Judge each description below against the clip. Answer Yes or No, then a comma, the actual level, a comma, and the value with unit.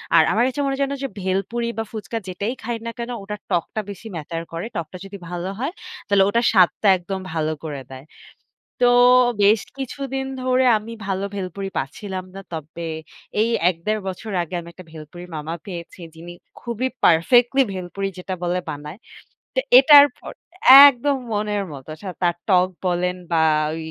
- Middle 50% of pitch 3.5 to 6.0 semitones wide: Yes, average, 5.2 semitones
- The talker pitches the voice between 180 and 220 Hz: Yes, high, 190 Hz